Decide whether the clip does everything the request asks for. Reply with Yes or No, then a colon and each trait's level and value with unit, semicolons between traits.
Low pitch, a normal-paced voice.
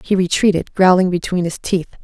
No: medium, 180 Hz; average, 175 wpm